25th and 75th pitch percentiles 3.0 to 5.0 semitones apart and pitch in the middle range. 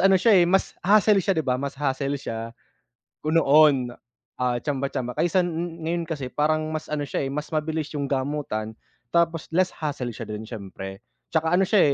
Yes: average, 4.0 semitones; medium, 150 Hz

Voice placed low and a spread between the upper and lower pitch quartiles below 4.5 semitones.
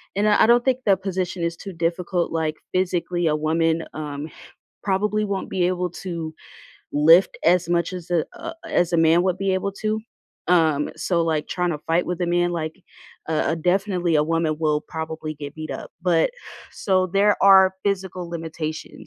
No: medium, 175 Hz; average, 2.7 semitones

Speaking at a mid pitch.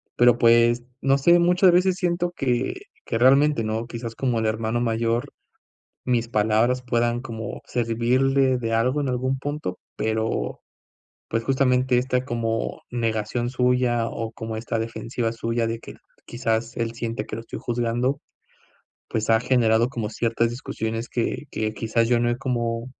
No: low, 120 Hz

